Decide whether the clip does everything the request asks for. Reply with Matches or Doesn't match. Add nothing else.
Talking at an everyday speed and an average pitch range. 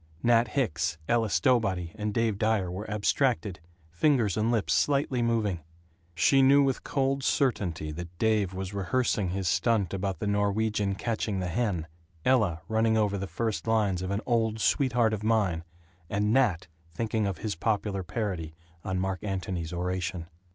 Matches